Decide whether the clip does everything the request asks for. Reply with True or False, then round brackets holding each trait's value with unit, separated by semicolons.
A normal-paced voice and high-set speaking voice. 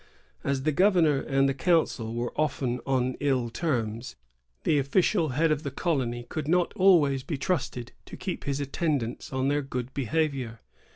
False (170 wpm; 140 Hz)